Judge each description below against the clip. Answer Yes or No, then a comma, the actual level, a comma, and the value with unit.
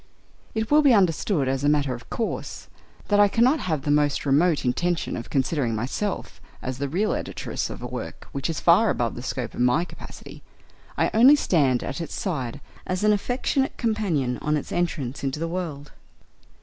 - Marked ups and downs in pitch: Yes, wide, 7.1 semitones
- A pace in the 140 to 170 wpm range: No, average, 190 wpm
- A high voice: No, medium, 155 Hz